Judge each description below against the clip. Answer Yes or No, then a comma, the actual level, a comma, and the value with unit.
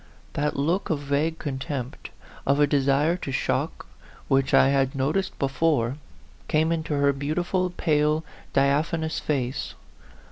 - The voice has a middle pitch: Yes, medium, 145 Hz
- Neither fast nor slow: No, slow, 130 wpm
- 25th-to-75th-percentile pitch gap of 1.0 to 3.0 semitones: Yes, narrow, 2.6 semitones